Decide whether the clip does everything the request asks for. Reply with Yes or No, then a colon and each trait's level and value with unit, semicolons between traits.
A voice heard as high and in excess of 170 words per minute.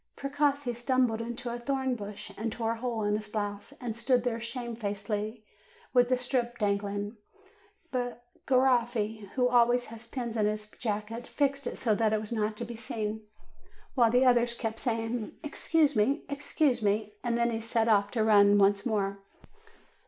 Yes: high, 230 Hz; average, 180 wpm